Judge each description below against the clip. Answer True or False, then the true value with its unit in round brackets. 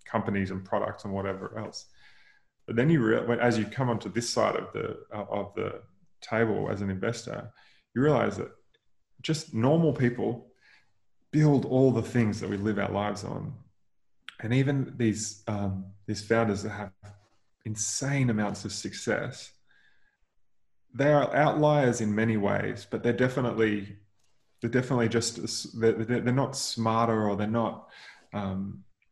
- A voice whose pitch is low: True (115 Hz)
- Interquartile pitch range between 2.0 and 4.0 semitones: True (3.1 semitones)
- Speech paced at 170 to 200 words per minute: False (145 wpm)